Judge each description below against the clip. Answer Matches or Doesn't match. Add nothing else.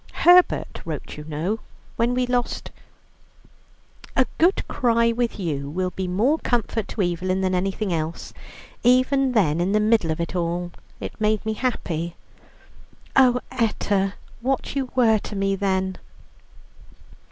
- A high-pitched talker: Matches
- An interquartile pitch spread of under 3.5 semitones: Doesn't match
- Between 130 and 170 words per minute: Matches